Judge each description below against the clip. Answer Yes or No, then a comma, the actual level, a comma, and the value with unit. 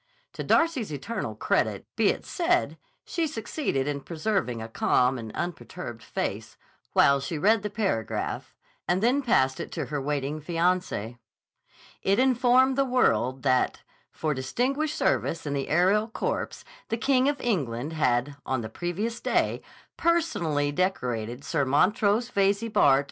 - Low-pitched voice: No, medium, 175 Hz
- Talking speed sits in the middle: Yes, average, 145 wpm